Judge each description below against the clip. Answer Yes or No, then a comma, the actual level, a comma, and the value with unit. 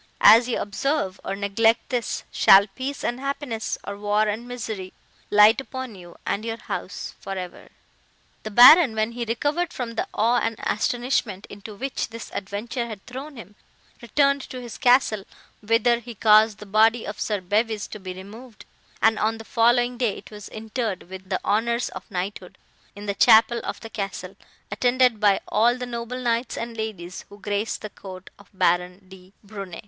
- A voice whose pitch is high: Yes, high, 220 Hz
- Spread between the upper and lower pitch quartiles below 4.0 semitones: Yes, average, 3.1 semitones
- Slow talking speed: No, average, 180 wpm